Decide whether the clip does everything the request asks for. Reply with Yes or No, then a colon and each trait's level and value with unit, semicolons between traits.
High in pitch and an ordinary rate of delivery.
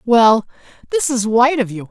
Yes: high, 235 Hz; average, 155 wpm